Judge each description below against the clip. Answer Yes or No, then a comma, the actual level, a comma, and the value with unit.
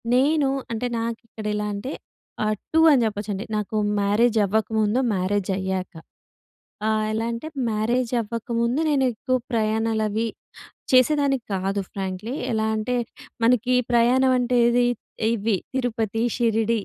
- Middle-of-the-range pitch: No, high, 225 Hz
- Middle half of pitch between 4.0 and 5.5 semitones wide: No, average, 2.7 semitones